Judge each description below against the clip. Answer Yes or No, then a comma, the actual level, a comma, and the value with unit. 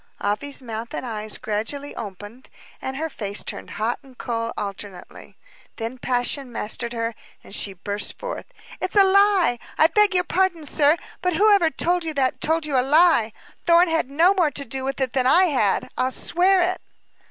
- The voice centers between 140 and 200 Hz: No, very high, 270 Hz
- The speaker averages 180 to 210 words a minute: Yes, average, 185 wpm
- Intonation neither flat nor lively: No, wide, 6.9 semitones